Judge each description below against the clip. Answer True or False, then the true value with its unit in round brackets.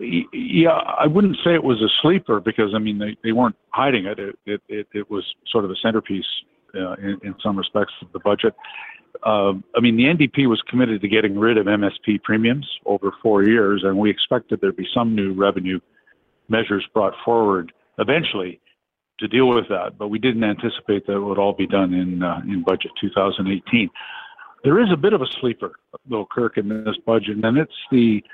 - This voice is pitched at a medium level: False (105 Hz)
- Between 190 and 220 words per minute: True (200 wpm)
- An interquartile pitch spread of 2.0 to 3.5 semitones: True (2.8 semitones)